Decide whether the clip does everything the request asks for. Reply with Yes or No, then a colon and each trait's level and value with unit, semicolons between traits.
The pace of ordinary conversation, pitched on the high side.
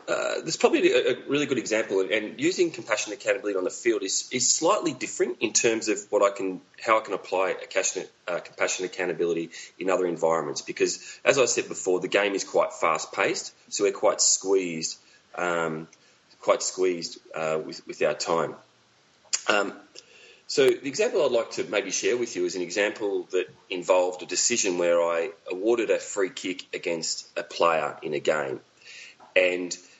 Yes: average, 175 wpm; very high, 345 Hz